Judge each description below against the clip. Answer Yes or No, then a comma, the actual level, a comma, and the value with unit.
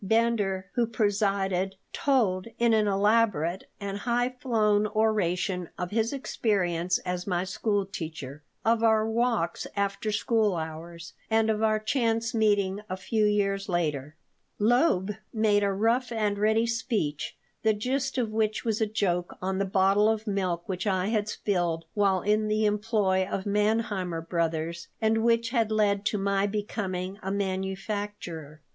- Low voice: No, high, 205 Hz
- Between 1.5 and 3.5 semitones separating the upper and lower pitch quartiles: Yes, average, 2.8 semitones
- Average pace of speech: Yes, average, 150 wpm